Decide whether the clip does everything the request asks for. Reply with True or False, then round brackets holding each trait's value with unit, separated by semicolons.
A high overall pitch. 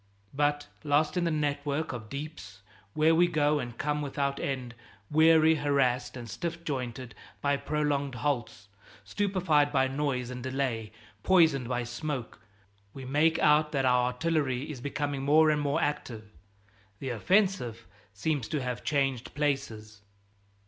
False (140 Hz)